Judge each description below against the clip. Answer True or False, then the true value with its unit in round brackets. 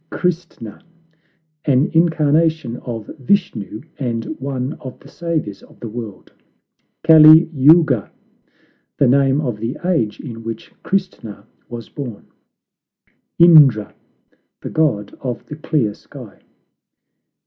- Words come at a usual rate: False (110 wpm)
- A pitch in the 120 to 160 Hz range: True (135 Hz)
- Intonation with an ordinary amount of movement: False (5.7 semitones)